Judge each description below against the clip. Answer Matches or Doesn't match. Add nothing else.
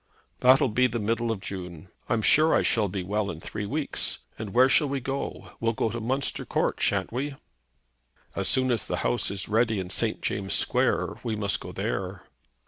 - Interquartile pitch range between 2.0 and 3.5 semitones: Doesn't match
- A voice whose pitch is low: Matches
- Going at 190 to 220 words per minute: Matches